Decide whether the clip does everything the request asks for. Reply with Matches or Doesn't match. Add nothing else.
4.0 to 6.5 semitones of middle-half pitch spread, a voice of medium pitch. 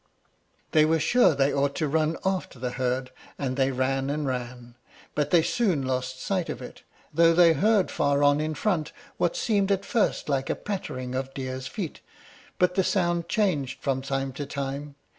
Matches